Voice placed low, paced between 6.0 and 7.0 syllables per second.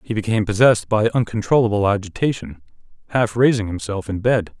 Yes: low, 110 Hz; 6.2 syllables/s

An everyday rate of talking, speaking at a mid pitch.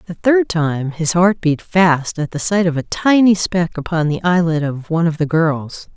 No: fast, 220 wpm; medium, 170 Hz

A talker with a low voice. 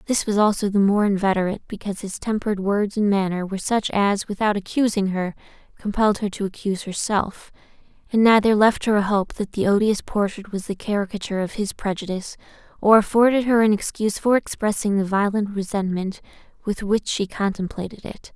No: high, 205 Hz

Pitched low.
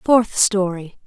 No: high, 200 Hz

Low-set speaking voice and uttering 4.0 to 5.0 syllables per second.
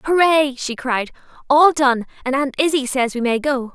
No: very high, 270 Hz; 4.6 syllables/s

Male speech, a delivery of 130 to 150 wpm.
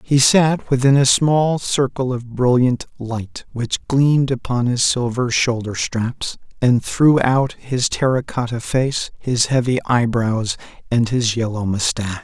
Yes: male; average, 145 wpm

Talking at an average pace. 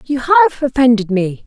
Yes: average, 165 wpm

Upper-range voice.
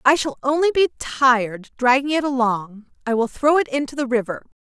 Yes: very high, 260 Hz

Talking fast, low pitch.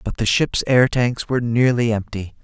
No: average, 195 wpm; low, 120 Hz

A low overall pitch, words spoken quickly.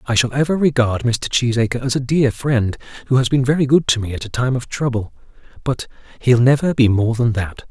Yes: low, 125 Hz; fast, 225 wpm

